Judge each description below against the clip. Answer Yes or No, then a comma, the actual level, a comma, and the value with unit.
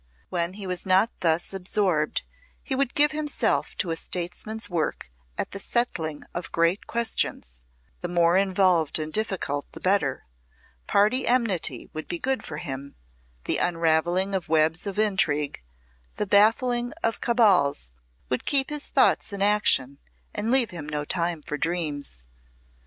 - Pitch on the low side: No, medium, 180 Hz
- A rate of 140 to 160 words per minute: Yes, average, 150 wpm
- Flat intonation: No, average, 5.3 semitones